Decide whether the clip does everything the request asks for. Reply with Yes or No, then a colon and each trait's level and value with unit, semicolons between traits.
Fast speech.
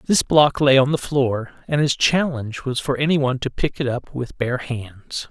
Yes: fast, 215 wpm